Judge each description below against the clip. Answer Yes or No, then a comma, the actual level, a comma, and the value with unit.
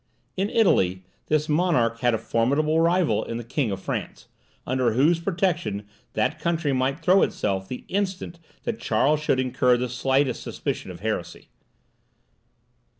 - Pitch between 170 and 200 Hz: No, medium, 140 Hz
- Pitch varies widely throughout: Yes, wide, 6.0 semitones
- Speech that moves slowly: No, average, 150 wpm